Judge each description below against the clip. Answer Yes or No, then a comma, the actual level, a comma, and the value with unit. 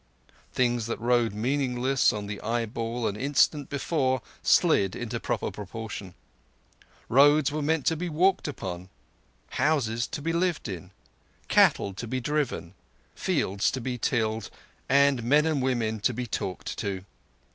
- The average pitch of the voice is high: No, low, 125 Hz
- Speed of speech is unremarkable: Yes, average, 145 wpm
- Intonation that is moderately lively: Yes, average, 4.6 semitones